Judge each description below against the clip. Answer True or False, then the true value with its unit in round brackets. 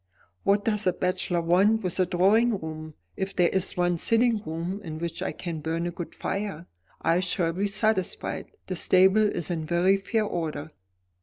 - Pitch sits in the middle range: True (180 Hz)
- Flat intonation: False (3.0 semitones)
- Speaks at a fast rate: False (180 wpm)